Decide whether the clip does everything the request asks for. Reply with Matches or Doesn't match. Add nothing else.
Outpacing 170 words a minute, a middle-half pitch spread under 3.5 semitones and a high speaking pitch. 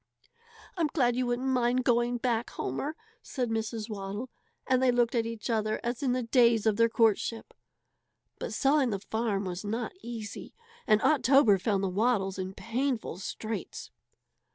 Doesn't match